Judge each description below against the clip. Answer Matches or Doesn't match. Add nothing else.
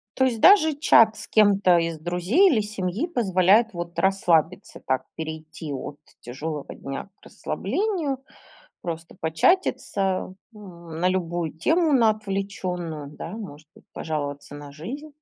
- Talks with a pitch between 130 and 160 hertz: Doesn't match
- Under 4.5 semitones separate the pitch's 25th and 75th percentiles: Doesn't match